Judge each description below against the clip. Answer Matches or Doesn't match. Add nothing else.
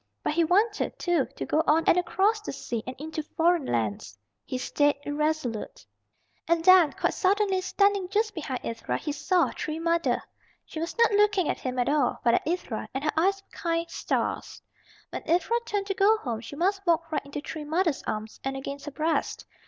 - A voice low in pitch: Doesn't match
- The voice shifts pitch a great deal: Doesn't match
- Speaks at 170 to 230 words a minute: Matches